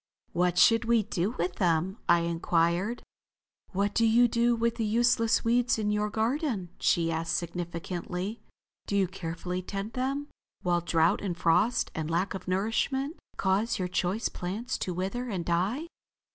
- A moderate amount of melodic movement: Yes, average, 4.8 semitones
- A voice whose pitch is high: Yes, high, 195 Hz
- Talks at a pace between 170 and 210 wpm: No, average, 160 wpm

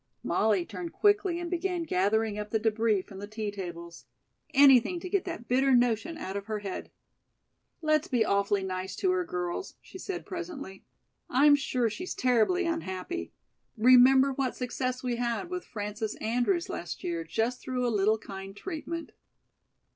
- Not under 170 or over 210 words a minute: No, average, 160 wpm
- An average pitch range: No, wide, 8.2 semitones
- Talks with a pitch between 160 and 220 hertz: No, high, 245 Hz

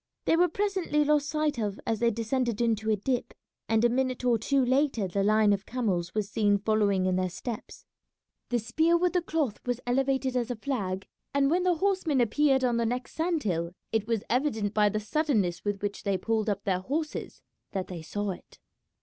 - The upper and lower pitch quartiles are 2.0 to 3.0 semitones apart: No, wide, 5.5 semitones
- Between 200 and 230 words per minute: Yes, fast, 205 wpm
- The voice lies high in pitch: Yes, high, 235 Hz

